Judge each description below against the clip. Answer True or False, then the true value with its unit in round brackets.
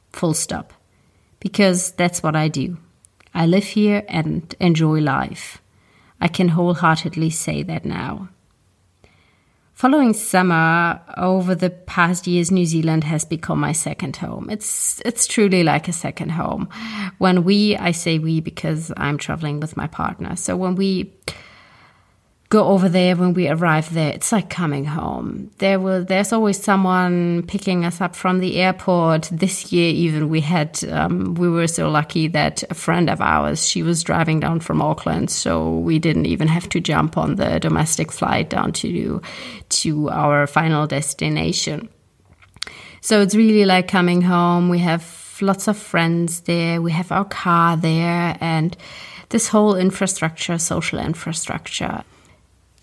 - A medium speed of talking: True (160 wpm)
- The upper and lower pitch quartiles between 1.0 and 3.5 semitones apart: True (2.8 semitones)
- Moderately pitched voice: True (170 Hz)